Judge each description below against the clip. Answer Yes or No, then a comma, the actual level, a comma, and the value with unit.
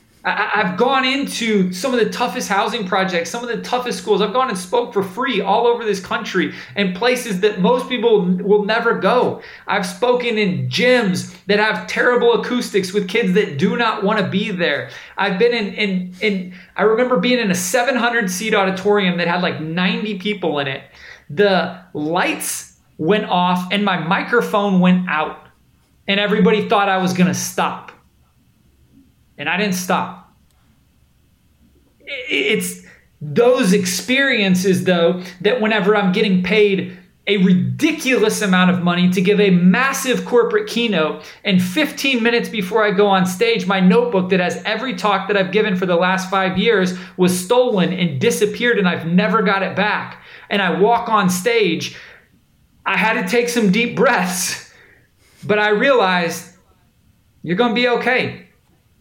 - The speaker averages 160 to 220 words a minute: Yes, average, 165 wpm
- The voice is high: Yes, high, 205 Hz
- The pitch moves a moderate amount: Yes, average, 4.0 semitones